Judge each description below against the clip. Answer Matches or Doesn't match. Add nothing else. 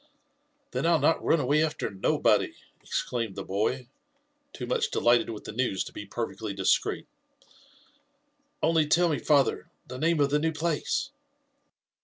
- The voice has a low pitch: Doesn't match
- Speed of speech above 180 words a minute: Doesn't match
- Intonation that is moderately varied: Doesn't match